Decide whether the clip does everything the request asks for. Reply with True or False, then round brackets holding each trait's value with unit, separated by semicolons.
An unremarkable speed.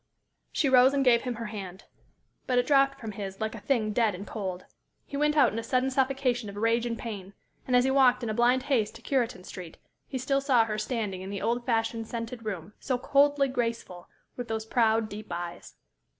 False (220 wpm)